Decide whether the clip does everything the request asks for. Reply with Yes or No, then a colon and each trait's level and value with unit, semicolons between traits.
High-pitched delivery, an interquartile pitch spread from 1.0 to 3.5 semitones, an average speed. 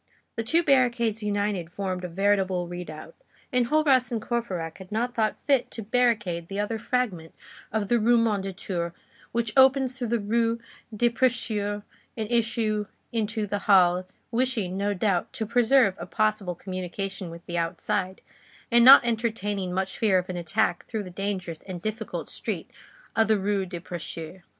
No: high, 205 Hz; average, 4.0 semitones; average, 160 wpm